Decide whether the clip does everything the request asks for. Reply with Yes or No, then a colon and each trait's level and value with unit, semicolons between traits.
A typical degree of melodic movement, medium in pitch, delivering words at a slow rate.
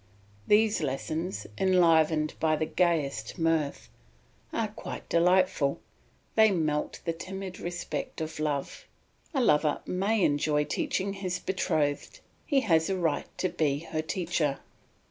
Yes: average, 3.7 semitones; medium, 165 Hz; slow, 125 wpm